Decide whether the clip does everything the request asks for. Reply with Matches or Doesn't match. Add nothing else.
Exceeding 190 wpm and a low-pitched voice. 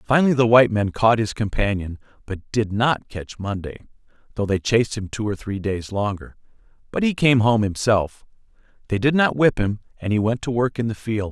Matches